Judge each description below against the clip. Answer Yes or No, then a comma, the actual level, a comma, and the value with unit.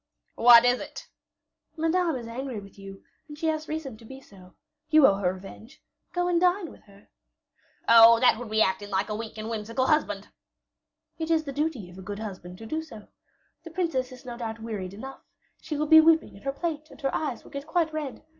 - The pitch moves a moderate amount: No, wide, 6.6 semitones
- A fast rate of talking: Yes, fast, 220 wpm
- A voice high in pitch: Yes, very high, 250 Hz